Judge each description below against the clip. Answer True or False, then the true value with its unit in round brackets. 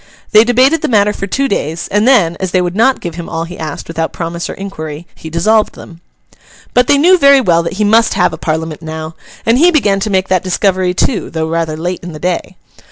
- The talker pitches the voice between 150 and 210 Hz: True (185 Hz)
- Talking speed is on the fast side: True (235 wpm)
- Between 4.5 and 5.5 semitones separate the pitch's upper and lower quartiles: True (5.0 semitones)